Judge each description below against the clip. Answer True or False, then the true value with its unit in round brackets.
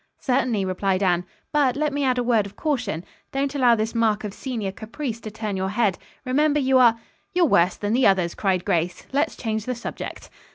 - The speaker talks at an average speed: False (210 wpm)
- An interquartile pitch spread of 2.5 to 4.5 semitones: False (5.1 semitones)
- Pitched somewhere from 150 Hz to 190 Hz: False (230 Hz)